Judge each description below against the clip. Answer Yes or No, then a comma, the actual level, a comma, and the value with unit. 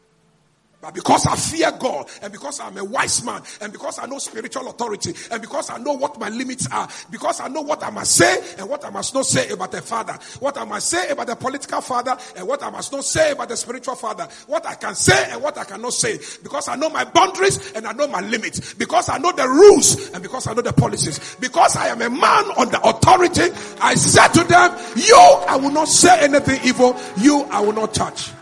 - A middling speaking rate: No, fast, 240 wpm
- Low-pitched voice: No, very high, 280 Hz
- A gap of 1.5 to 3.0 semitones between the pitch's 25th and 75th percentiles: No, average, 4.1 semitones